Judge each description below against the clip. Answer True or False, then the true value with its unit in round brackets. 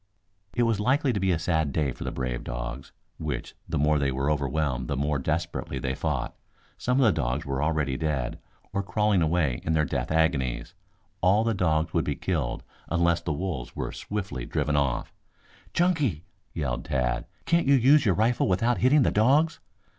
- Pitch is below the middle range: True (80 Hz)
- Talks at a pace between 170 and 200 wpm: True (190 wpm)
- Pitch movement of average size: False (7.3 semitones)